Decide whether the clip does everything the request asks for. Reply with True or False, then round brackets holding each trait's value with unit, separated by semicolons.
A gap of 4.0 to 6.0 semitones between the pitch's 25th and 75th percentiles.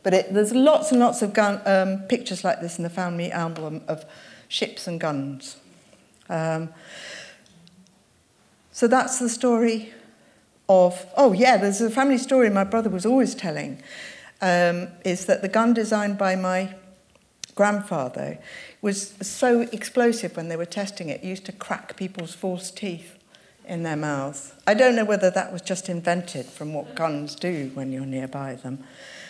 True (4.4 semitones)